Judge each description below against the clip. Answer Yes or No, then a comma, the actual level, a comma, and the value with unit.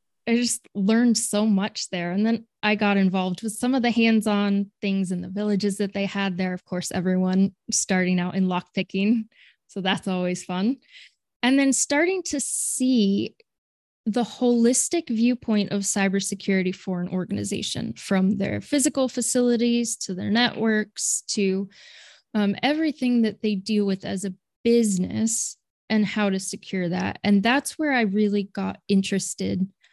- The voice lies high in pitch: Yes, high, 205 Hz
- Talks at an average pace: Yes, average, 155 wpm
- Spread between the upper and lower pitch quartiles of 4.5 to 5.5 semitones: No, average, 3.5 semitones